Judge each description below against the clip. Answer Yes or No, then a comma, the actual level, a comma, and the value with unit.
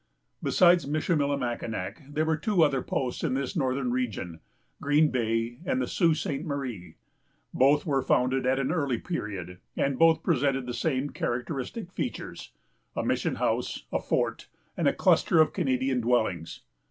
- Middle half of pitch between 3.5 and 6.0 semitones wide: Yes, average, 4.1 semitones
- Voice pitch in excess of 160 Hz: No, low, 135 Hz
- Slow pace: No, average, 150 wpm